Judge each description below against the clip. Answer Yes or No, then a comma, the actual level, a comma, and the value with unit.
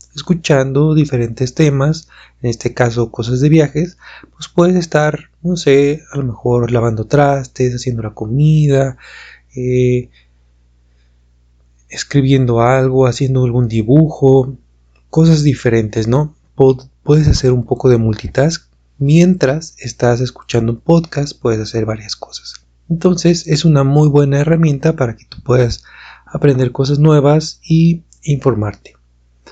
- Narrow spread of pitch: No, average, 4.2 semitones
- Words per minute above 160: No, slow, 125 wpm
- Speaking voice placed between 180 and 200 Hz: No, low, 130 Hz